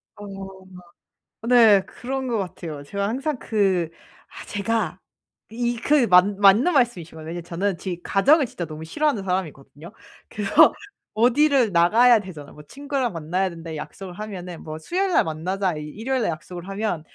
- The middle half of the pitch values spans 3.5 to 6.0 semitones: Yes, wide, 5.6 semitones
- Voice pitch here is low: No, high, 195 Hz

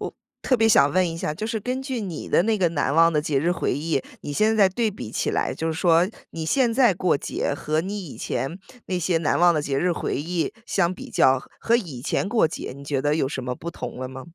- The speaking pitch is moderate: Yes, medium, 170 Hz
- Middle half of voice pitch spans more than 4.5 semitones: Yes, wide, 5.4 semitones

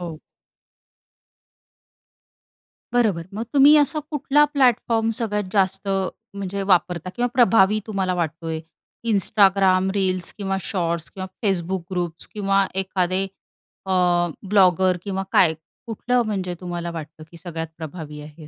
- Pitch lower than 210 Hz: Yes, high, 190 Hz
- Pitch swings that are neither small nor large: Yes, average, 3.2 semitones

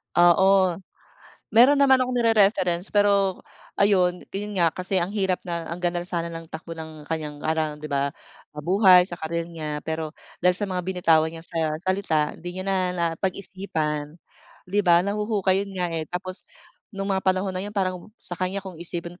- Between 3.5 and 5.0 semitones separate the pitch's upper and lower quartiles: No, average, 2.8 semitones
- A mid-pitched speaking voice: Yes, medium, 180 Hz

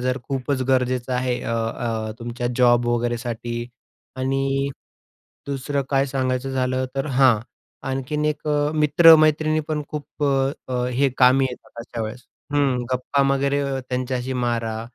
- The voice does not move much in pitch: Yes, narrow, 2.3 semitones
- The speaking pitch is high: No, low, 130 Hz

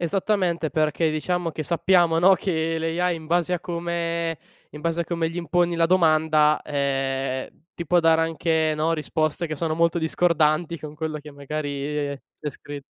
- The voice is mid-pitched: Yes, medium, 160 Hz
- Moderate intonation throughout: No, narrow, 2.0 semitones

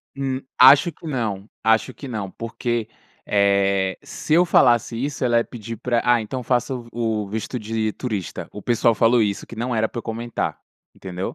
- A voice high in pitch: No, low, 115 Hz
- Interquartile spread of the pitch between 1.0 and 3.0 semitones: Yes, narrow, 2.6 semitones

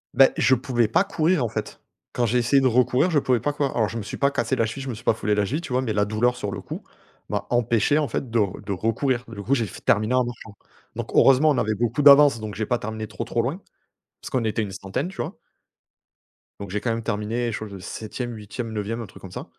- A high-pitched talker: No, low, 115 Hz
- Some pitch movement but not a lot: Yes, average, 3.5 semitones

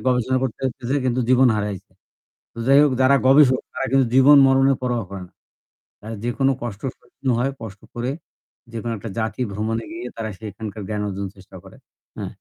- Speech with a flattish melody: No, average, 3.7 semitones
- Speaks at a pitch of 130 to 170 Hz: No, low, 120 Hz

